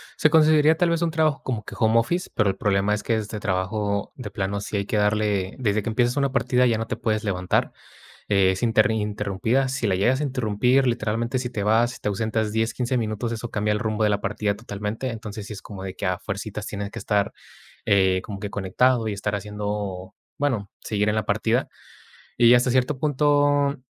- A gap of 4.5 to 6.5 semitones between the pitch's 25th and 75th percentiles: No, average, 3.4 semitones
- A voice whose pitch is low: Yes, low, 110 Hz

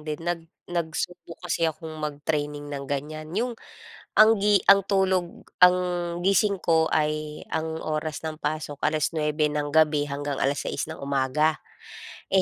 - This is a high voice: No, medium, 155 Hz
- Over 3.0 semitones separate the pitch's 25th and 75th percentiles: No, average, 2.7 semitones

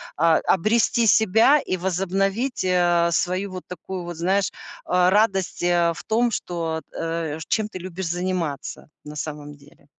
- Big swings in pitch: No, average, 2.7 semitones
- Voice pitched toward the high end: No, medium, 180 Hz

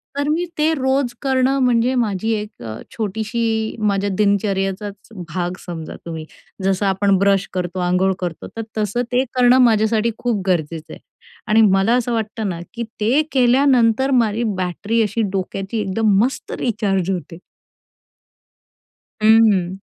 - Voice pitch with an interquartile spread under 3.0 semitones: No, average, 3.7 semitones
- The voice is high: Yes, high, 215 Hz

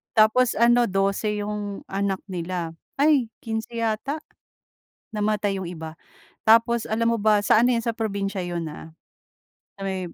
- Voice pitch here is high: Yes, high, 210 Hz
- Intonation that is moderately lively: Yes, average, 3.0 semitones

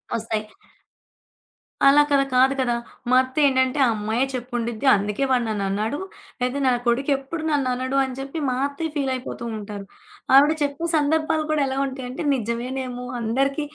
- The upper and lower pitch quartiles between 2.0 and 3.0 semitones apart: Yes, average, 2.7 semitones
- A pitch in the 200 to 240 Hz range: No, very high, 260 Hz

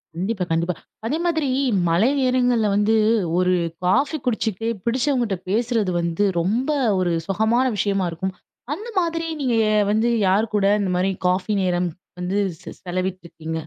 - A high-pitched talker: Yes, high, 205 Hz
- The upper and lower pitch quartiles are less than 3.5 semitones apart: No, average, 4.9 semitones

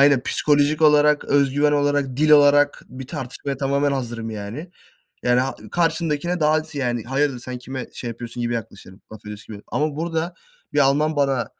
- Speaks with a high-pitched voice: No, medium, 140 Hz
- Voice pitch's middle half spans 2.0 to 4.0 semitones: Yes, average, 3.3 semitones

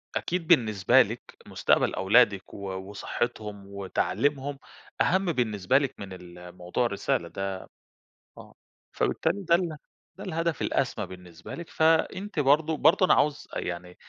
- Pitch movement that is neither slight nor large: No, wide, 8.8 semitones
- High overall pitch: No, low, 120 Hz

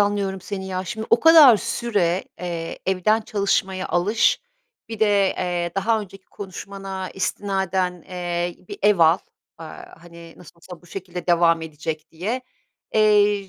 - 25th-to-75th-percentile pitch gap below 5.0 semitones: Yes, average, 2.9 semitones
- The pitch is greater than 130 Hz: Yes, high, 190 Hz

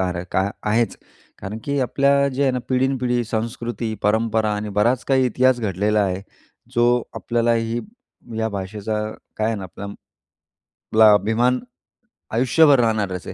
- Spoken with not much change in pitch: No, average, 3.1 semitones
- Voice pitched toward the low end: Yes, low, 115 Hz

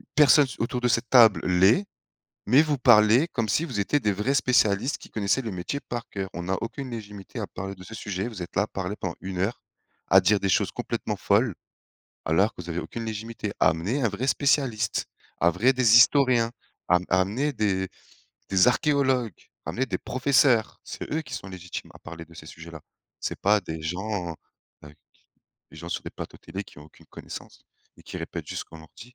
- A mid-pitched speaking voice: No, low, 105 Hz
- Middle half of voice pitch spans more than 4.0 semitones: Yes, average, 5.1 semitones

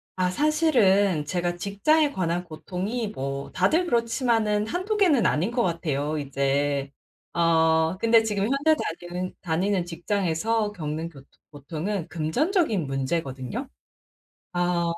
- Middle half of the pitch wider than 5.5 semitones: Yes, wide, 6.1 semitones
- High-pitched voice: No, medium, 180 Hz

